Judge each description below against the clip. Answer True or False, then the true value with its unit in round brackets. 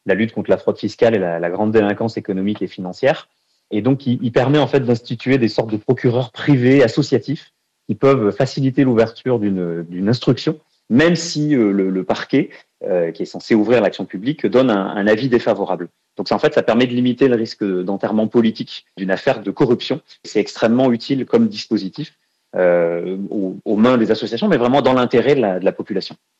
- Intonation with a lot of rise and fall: False (4.5 semitones)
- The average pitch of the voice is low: True (115 Hz)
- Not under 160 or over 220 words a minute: True (200 wpm)